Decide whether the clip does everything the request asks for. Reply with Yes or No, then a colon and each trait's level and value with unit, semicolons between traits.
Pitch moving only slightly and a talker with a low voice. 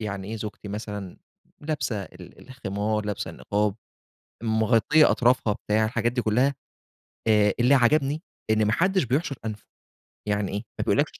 No: average, 3.6 semitones; low, 110 Hz